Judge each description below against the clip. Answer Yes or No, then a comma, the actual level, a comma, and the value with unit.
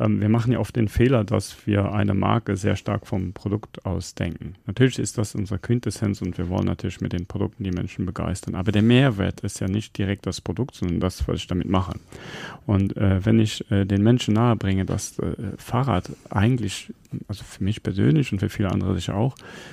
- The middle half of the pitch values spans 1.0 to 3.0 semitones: Yes, average, 2.7 semitones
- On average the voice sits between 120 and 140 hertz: No, low, 105 Hz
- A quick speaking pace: Yes, fast, 205 wpm